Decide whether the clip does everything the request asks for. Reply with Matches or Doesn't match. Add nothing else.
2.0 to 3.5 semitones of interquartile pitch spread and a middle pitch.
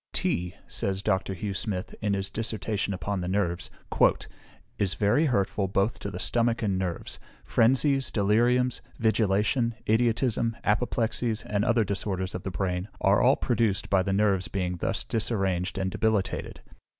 Doesn't match